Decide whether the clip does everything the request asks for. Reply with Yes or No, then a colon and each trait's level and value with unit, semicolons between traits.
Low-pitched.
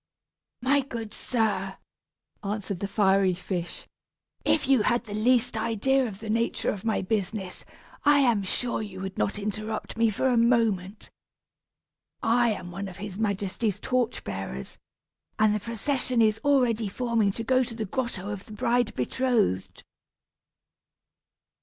No: high, 215 Hz